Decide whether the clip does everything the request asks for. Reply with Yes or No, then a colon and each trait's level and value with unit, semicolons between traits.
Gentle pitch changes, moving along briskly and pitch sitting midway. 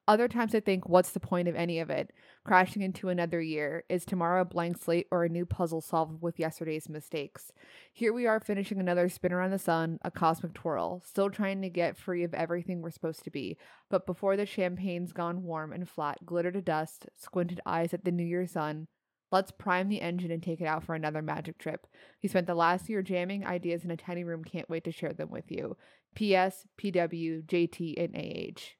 Yes: narrow, 1.9 semitones; fast, 215 wpm; medium, 175 Hz